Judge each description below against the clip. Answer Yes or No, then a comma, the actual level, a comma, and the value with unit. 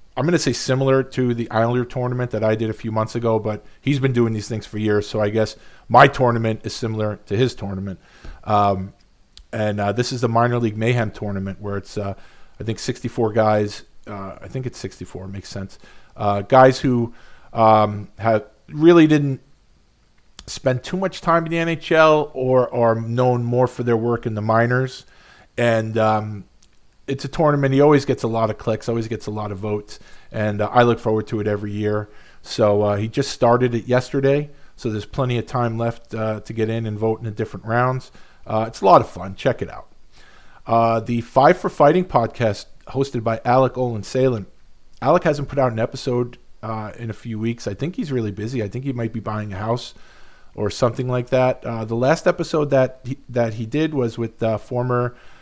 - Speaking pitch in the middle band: No, low, 115 Hz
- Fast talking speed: Yes, fast, 210 wpm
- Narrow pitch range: No, average, 3.2 semitones